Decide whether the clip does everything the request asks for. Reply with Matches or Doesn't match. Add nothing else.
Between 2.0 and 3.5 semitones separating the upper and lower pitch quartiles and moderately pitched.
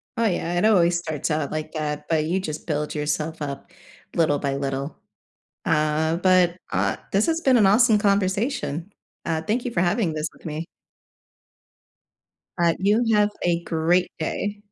Doesn't match